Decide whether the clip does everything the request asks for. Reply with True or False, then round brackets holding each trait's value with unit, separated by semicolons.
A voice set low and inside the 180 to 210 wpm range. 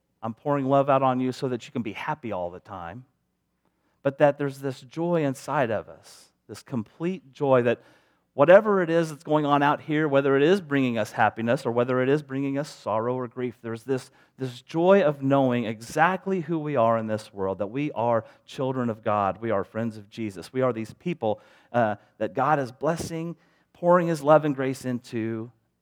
True (130 Hz; 205 wpm)